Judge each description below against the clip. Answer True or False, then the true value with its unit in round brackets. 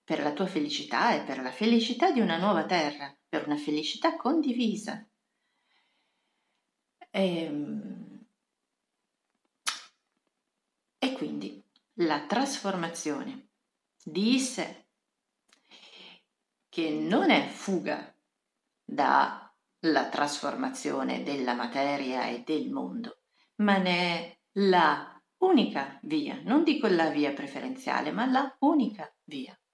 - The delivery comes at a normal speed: False (100 wpm)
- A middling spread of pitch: False (9.0 semitones)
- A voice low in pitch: False (205 Hz)